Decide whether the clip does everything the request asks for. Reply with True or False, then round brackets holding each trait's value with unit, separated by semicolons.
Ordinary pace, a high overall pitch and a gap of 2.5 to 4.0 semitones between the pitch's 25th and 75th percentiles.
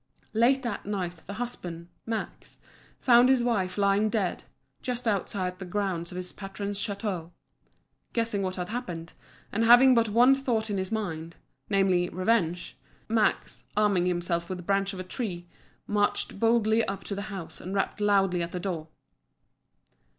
True (160 wpm; 200 Hz; 3.7 semitones)